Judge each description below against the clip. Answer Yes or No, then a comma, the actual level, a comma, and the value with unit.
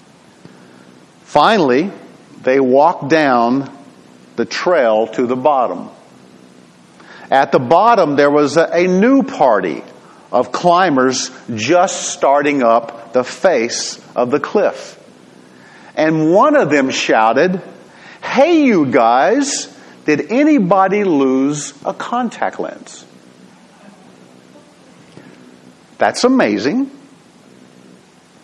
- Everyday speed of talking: No, slow, 90 wpm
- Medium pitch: No, low, 130 Hz